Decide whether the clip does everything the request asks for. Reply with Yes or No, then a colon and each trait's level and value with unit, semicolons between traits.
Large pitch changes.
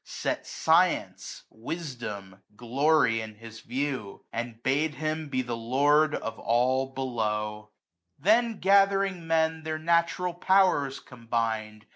Yes: wide, 5.8 semitones